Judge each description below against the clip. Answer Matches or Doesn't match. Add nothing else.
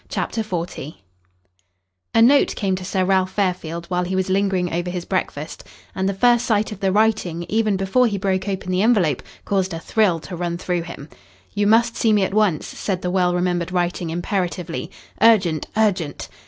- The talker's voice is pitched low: Doesn't match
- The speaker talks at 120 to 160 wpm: Doesn't match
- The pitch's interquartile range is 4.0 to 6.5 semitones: Doesn't match